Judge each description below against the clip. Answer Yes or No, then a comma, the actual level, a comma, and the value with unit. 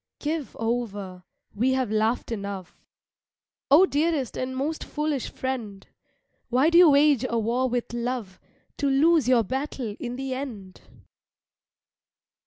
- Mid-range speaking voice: No, very high, 255 Hz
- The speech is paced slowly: Yes, slow, 130 wpm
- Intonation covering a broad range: No, average, 4.0 semitones